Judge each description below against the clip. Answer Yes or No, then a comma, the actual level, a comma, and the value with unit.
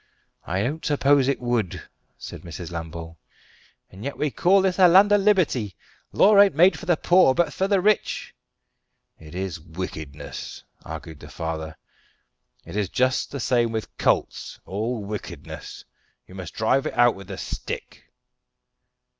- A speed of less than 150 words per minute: No, average, 155 wpm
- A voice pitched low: Yes, low, 115 Hz